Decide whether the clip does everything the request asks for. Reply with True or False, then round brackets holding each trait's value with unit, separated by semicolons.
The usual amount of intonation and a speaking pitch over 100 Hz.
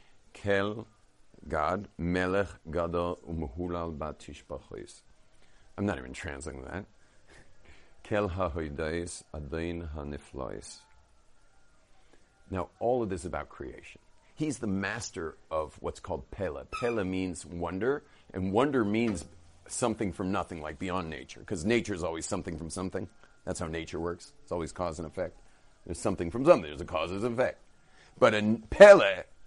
False (3.5 semitones; 90 Hz)